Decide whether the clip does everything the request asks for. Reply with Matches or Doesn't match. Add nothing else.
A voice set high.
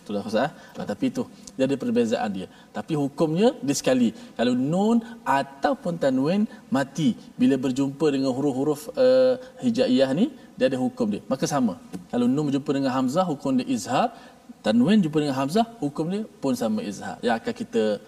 Matches